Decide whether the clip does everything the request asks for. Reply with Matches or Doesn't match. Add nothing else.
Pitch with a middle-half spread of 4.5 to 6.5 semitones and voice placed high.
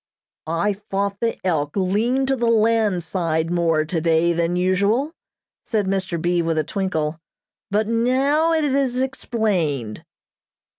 Matches